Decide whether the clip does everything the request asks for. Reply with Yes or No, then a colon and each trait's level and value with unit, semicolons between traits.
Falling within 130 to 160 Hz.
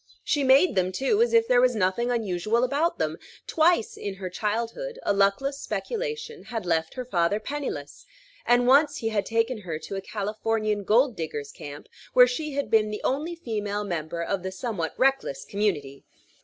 No: high, 220 Hz